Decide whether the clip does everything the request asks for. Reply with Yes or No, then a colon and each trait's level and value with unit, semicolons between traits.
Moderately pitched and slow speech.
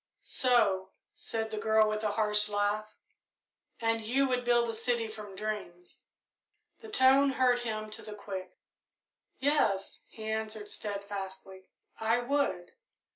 No: high, 215 Hz; slow, 130 wpm